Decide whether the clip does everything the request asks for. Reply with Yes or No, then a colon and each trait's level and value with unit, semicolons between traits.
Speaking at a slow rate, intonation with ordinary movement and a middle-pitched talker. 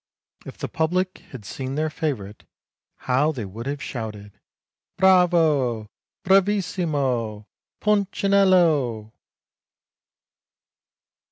No: slow, 85 wpm; wide, 7.7 semitones; medium, 145 Hz